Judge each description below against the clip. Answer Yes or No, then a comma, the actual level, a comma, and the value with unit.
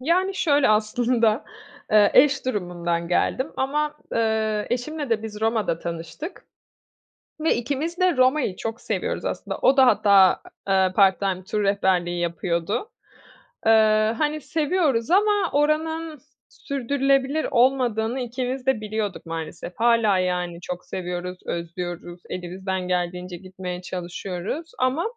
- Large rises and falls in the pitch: Yes, wide, 6.9 semitones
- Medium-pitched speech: No, high, 220 Hz